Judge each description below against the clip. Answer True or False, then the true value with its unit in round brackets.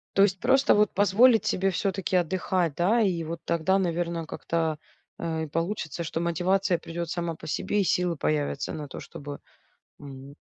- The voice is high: False (170 Hz)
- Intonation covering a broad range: False (3.0 semitones)